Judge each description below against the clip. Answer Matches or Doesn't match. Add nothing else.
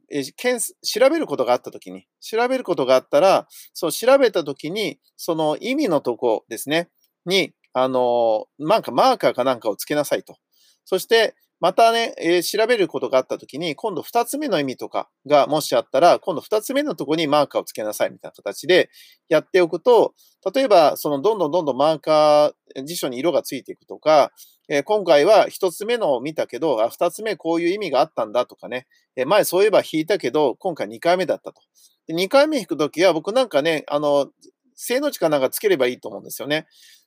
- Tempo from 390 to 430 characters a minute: Matches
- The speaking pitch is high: Matches